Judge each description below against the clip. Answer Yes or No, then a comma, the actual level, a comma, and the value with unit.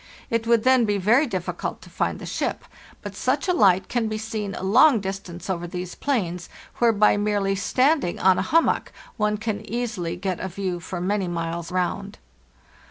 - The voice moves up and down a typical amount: Yes, average, 4.0 semitones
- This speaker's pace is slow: No, average, 190 wpm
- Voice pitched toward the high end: Yes, high, 200 Hz